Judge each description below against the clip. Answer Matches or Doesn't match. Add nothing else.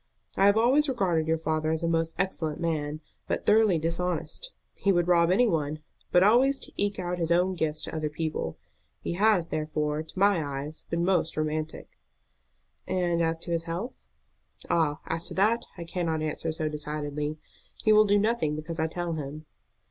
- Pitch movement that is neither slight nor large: Matches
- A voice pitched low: Doesn't match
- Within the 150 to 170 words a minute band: Doesn't match